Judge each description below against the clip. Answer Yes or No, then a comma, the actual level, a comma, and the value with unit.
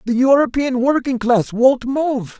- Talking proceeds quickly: No, average, 150 wpm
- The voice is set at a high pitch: Yes, very high, 250 Hz